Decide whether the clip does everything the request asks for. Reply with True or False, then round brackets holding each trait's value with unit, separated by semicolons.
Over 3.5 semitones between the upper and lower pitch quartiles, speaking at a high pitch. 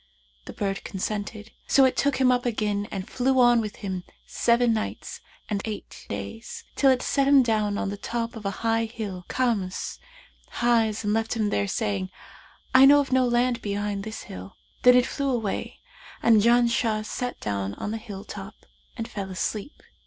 False (3.2 semitones; 220 Hz)